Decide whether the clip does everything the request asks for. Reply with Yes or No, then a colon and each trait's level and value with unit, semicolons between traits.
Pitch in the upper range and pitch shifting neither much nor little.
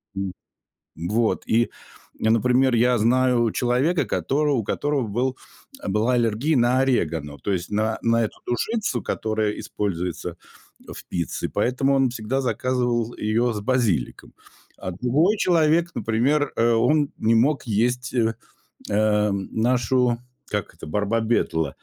No: low, 120 Hz; average, 3.3 semitones